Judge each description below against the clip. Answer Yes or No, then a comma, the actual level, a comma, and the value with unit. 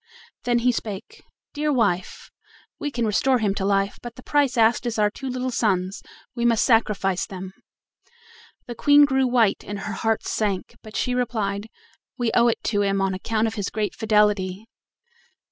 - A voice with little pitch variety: No, average, 3.4 semitones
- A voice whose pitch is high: Yes, high, 220 Hz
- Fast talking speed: No, average, 180 wpm